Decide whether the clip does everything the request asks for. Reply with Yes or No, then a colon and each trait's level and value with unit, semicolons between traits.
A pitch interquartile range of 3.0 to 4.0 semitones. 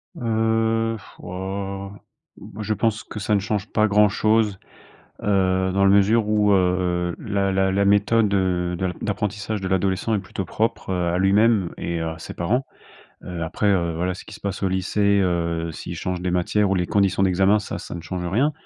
No: narrow, 2.5 semitones